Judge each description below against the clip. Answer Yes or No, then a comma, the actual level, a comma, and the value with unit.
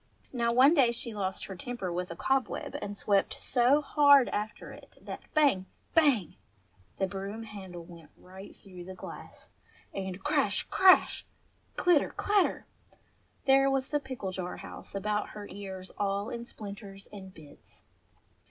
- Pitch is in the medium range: No, high, 205 Hz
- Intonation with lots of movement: Yes, wide, 5.9 semitones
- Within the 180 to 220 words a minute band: No, average, 150 wpm